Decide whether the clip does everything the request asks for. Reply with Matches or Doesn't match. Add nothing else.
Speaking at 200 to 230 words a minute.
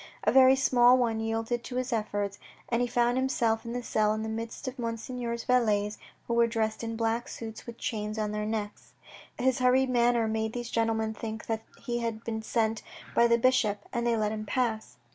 Matches